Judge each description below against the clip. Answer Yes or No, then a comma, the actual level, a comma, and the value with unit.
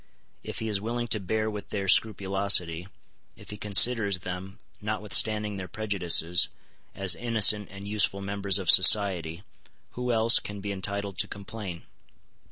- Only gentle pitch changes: Yes, narrow, 2.1 semitones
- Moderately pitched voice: No, low, 100 Hz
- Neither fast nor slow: Yes, average, 145 wpm